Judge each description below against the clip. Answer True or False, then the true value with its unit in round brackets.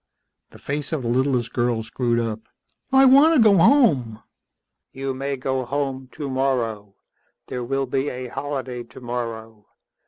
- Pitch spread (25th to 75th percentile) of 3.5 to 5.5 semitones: False (3.0 semitones)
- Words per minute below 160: True (145 wpm)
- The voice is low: True (130 Hz)